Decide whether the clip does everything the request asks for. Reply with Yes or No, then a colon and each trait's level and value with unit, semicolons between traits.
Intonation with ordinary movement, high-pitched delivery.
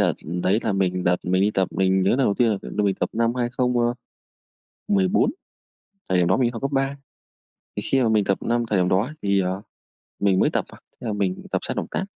No: average, 4.4 semitones; low, 105 Hz